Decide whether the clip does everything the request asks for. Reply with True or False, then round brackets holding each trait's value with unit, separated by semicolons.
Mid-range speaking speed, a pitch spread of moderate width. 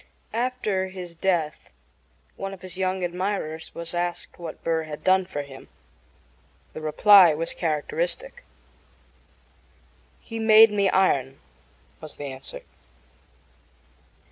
False (115 wpm; 3.8 semitones)